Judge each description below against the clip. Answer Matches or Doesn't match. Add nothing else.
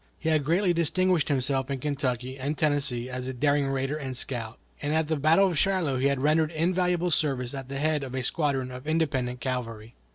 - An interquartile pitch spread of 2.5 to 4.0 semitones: Matches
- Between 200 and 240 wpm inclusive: Matches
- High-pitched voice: Doesn't match